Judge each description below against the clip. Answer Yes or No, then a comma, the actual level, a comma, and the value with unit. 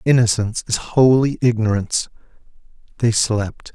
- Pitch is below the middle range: Yes, low, 115 Hz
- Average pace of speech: No, slow, 95 wpm